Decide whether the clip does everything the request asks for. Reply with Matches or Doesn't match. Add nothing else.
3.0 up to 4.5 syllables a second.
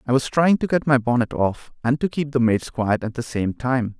Doesn't match